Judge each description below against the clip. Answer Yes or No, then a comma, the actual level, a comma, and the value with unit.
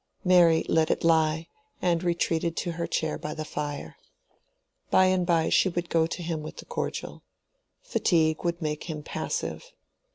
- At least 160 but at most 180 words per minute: Yes, average, 165 wpm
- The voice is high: No, medium, 165 Hz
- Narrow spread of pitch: Yes, narrow, 1.7 semitones